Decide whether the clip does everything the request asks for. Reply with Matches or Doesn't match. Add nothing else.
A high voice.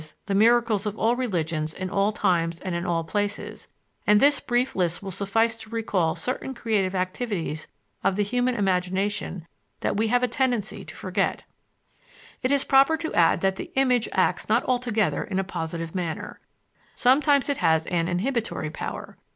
Matches